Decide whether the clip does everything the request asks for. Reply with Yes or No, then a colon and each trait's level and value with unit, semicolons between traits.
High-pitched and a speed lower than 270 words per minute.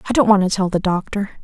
No: high, 195 Hz; fast, 295 wpm